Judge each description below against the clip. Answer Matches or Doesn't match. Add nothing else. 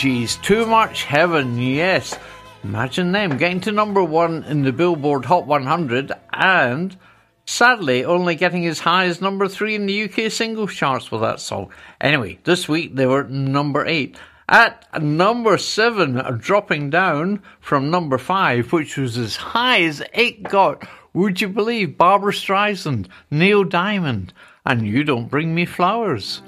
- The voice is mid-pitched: Matches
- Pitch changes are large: Matches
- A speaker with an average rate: Matches